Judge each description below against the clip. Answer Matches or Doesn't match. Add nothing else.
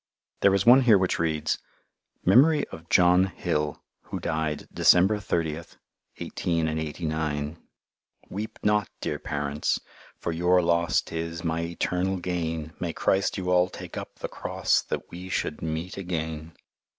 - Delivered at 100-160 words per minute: Matches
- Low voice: Matches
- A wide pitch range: Doesn't match